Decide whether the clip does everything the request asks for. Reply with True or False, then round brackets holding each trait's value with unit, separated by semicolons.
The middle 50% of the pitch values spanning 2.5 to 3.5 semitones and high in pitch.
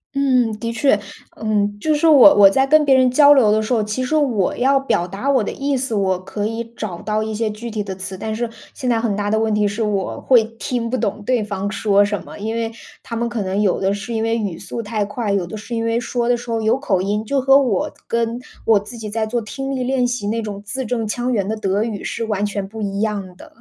True (3.1 semitones; 220 Hz)